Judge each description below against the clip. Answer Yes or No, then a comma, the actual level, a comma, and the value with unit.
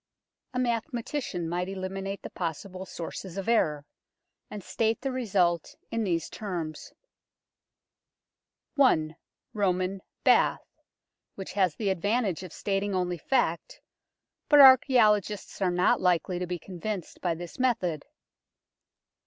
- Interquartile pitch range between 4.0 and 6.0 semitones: No, average, 3.6 semitones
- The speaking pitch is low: No, high, 190 Hz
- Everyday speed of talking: No, slow, 120 wpm